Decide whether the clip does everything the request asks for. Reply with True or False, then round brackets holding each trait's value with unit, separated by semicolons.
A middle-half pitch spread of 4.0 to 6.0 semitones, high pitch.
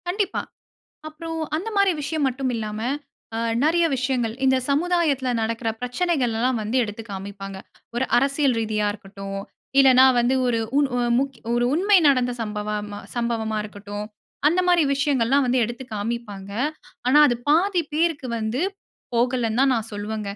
True (4.9 semitones; 250 Hz)